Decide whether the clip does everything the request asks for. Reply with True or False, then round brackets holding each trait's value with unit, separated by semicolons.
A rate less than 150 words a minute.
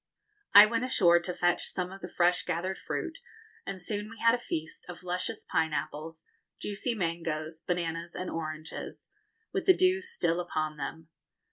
False (160 wpm)